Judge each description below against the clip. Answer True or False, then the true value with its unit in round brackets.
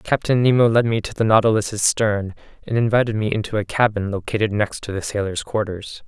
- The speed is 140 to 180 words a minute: False (200 wpm)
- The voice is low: True (110 Hz)